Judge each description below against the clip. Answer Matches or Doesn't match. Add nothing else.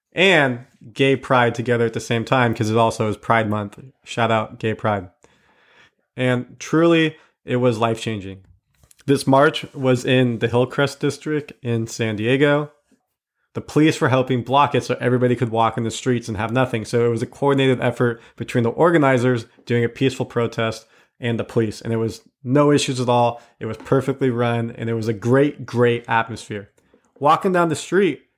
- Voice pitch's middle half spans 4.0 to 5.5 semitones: Doesn't match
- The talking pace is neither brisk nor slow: Matches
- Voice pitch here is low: Matches